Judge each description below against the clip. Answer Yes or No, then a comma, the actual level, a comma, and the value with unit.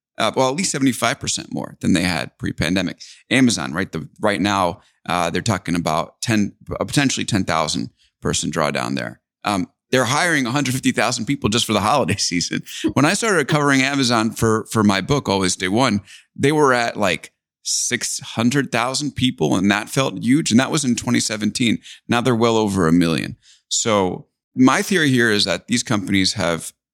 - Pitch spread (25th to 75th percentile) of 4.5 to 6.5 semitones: Yes, average, 5.2 semitones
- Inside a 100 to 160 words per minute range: No, average, 190 wpm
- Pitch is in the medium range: No, low, 115 Hz